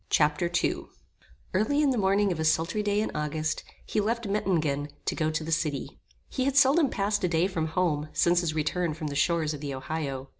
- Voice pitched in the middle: Yes, medium, 165 Hz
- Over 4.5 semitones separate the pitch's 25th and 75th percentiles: Yes, average, 4.9 semitones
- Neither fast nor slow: No, fast, 215 wpm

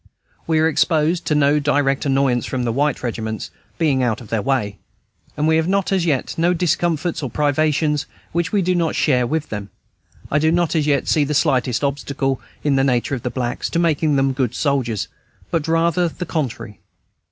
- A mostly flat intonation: No, average, 3.7 semitones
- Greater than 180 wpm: Yes, average, 195 wpm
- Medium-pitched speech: Yes, medium, 145 Hz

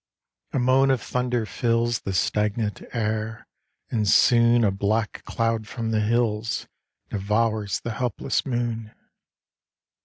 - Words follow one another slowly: Yes, slow, 120 wpm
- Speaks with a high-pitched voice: No, low, 115 Hz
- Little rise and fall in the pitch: Yes, narrow, 1.9 semitones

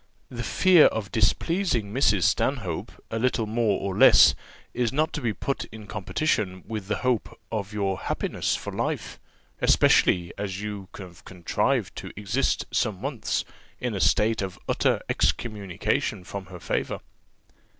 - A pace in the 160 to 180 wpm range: No, average, 150 wpm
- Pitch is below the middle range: Yes, low, 105 Hz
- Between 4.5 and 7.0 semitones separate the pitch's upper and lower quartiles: No, average, 3.9 semitones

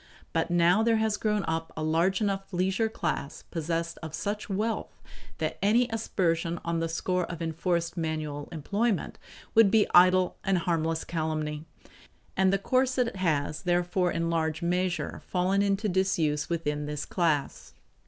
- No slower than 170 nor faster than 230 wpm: No, average, 150 wpm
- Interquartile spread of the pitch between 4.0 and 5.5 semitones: No, average, 3.3 semitones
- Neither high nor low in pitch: Yes, medium, 175 Hz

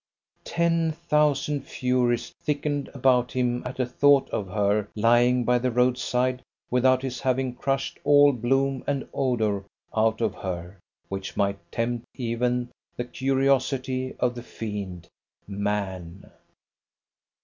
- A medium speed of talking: No, slow, 125 wpm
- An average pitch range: Yes, average, 3.3 semitones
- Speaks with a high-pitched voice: No, low, 125 Hz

